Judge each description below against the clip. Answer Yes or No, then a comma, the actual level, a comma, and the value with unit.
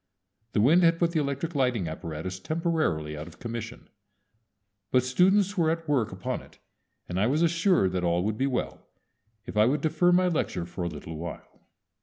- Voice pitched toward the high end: No, low, 125 Hz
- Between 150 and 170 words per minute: No, average, 190 wpm